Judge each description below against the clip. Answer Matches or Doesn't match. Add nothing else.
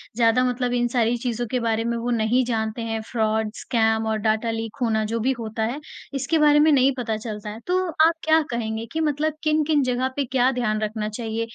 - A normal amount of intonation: Matches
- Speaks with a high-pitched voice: Matches